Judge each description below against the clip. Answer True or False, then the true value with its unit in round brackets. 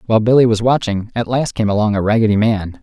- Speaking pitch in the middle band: False (110 Hz)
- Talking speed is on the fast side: True (235 wpm)